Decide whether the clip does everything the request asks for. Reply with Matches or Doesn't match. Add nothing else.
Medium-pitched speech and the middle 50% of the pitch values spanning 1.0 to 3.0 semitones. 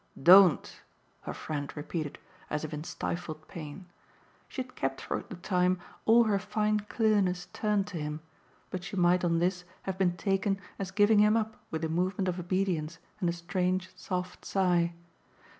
Matches